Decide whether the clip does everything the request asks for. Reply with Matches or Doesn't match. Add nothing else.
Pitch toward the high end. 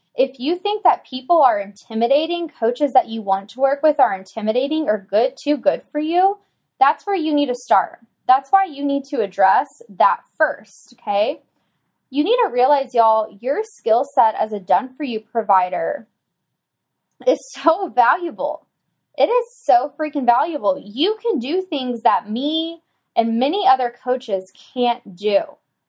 Matches